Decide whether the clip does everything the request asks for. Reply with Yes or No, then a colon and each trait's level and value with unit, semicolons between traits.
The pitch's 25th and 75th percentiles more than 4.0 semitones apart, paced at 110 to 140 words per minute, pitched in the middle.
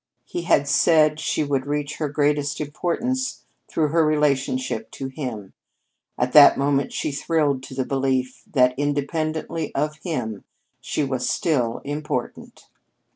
No: narrow, 2.5 semitones; slow, 135 wpm; medium, 145 Hz